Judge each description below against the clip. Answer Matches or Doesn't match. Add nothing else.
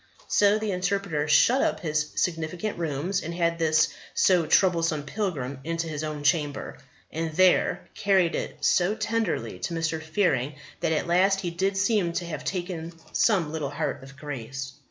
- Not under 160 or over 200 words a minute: Matches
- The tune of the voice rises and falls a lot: Doesn't match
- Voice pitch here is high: Doesn't match